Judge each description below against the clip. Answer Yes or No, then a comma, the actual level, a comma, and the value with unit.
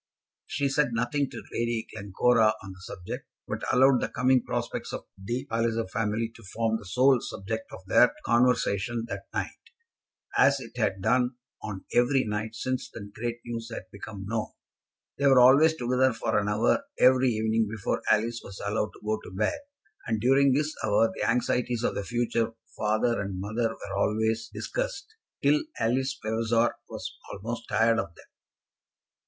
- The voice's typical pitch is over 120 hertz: No, low, 115 Hz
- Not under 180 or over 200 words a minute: No, average, 170 wpm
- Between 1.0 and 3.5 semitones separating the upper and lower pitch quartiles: Yes, average, 2.7 semitones